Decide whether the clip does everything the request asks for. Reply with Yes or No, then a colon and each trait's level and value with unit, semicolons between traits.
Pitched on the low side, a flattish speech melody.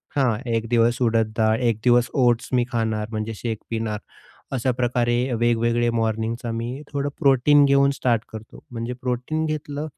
Yes: low, 120 Hz; narrow, 2.2 semitones